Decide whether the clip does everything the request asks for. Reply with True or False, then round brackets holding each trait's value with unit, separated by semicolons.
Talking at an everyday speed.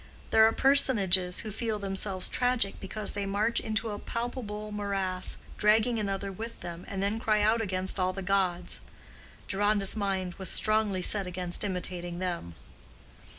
True (150 wpm)